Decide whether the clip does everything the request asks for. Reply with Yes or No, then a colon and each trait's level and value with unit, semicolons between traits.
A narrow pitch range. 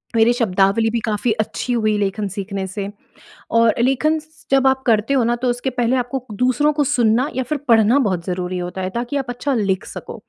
No: average, 4.1 semitones